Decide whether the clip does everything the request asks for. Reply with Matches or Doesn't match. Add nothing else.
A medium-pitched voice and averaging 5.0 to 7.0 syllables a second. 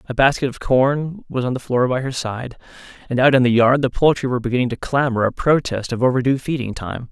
Doesn't match